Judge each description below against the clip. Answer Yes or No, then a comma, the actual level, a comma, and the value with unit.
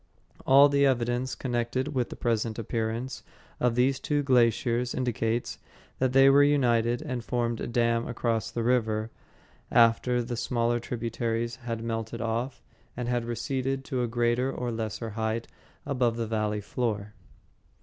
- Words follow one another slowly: No, average, 150 wpm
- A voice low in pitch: Yes, low, 120 Hz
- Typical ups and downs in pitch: No, narrow, 1.7 semitones